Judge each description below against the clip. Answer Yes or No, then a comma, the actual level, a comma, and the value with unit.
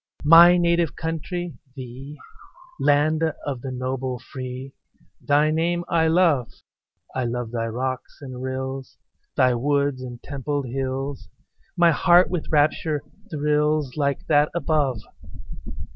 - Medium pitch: Yes, medium, 145 Hz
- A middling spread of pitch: Yes, average, 3.4 semitones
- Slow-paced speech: Yes, slow, 120 wpm